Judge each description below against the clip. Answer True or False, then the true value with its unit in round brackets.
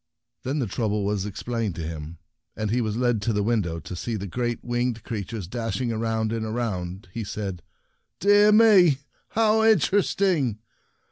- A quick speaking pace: False (175 wpm)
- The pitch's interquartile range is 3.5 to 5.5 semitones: True (3.8 semitones)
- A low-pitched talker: True (115 Hz)